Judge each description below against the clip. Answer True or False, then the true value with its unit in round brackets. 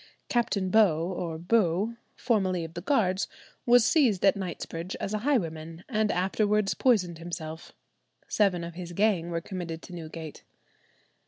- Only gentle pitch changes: False (4.1 semitones)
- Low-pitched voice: False (185 Hz)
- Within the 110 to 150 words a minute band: True (145 wpm)